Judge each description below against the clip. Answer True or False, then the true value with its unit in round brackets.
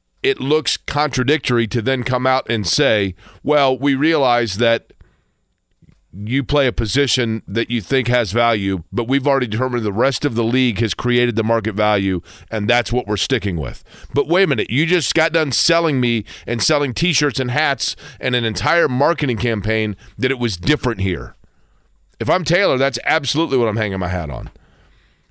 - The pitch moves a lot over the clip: False (4.0 semitones)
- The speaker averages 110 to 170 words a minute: False (185 wpm)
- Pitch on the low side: True (120 Hz)